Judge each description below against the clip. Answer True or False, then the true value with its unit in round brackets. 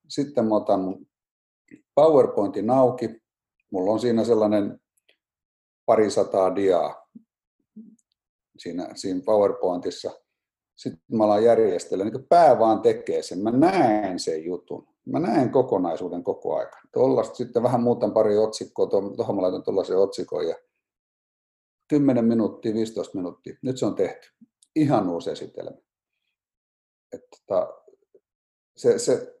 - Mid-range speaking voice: True (145 Hz)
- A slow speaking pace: False (115 wpm)